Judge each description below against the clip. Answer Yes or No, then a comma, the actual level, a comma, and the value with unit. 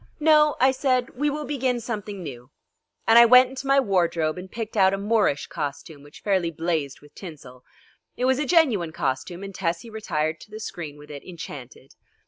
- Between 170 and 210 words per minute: Yes, average, 190 wpm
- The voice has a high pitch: Yes, high, 195 Hz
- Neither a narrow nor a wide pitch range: No, wide, 8.2 semitones